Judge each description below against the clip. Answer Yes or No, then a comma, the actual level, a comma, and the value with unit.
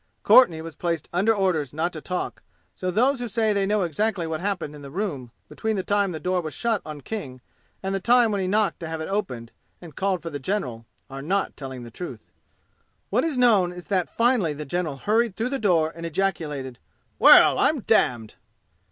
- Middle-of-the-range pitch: Yes, medium, 180 Hz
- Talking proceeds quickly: Yes, fast, 215 wpm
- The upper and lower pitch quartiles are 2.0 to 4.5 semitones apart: No, average, 5.2 semitones